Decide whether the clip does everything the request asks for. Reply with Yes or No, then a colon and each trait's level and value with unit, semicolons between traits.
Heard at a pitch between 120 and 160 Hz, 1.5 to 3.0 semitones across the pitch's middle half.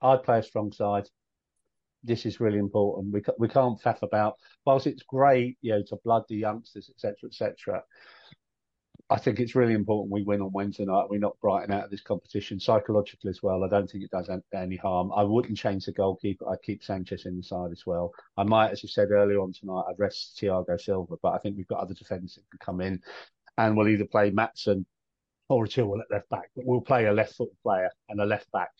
No: low, 105 Hz; narrow, 2.4 semitones